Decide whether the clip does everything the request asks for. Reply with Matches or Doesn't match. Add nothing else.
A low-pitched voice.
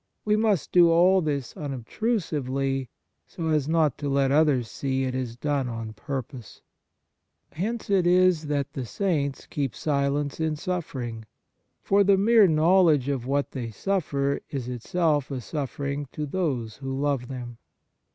Doesn't match